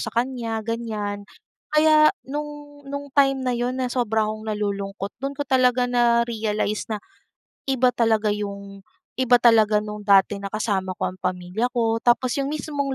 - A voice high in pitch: Yes, high, 230 Hz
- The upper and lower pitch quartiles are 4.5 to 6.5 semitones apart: No, average, 3.8 semitones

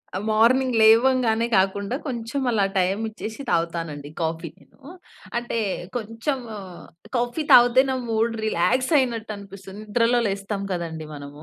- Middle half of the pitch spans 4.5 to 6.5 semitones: No, average, 4.0 semitones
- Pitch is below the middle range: No, high, 220 Hz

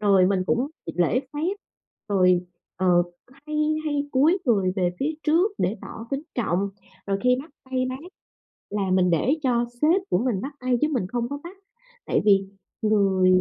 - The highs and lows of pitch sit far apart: Yes, wide, 7.0 semitones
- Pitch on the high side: Yes, high, 235 Hz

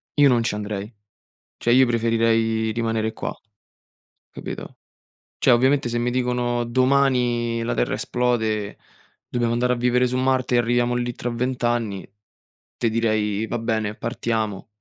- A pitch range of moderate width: No, narrow, 1.7 semitones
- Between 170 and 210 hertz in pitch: No, low, 120 Hz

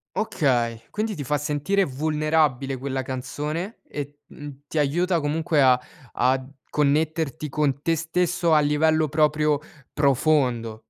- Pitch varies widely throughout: No, average, 2.7 semitones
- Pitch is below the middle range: No, medium, 150 Hz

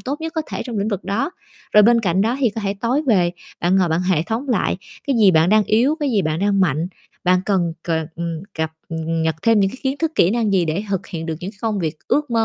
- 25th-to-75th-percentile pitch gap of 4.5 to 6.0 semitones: Yes, average, 5.1 semitones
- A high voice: Yes, high, 200 Hz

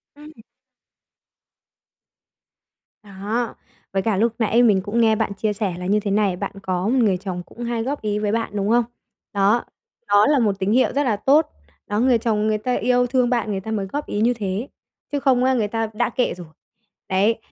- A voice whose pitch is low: No, high, 220 Hz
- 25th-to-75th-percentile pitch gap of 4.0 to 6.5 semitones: No, average, 3.3 semitones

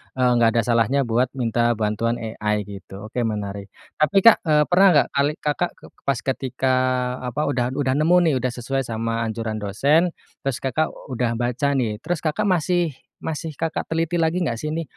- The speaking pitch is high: No, low, 130 Hz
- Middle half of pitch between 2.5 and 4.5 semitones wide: No, average, 5.0 semitones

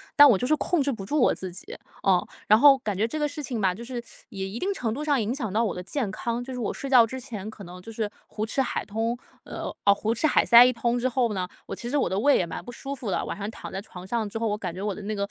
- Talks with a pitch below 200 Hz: No, high, 225 Hz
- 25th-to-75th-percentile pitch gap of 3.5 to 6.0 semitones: Yes, average, 4.3 semitones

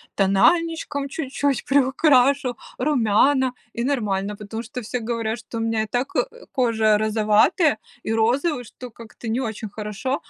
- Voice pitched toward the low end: No, high, 235 Hz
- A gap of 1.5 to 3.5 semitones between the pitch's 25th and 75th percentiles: No, average, 3.9 semitones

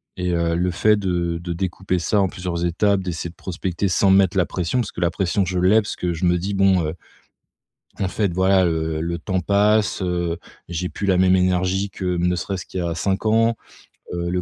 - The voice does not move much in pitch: Yes, narrow, 2.0 semitones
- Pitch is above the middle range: No, very low, 90 Hz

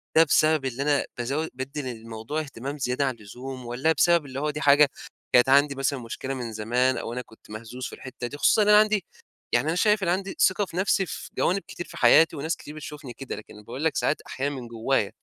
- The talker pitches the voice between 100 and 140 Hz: Yes, low, 135 Hz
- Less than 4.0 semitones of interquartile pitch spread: No, average, 4.3 semitones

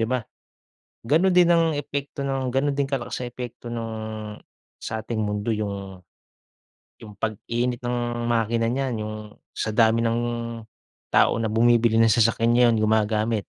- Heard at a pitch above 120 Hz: No, low, 115 Hz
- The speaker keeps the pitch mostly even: Yes, narrow, 2.3 semitones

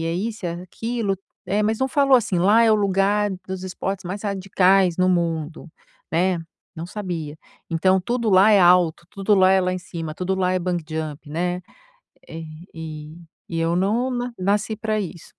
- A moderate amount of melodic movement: Yes, average, 3.3 semitones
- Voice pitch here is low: No, medium, 185 Hz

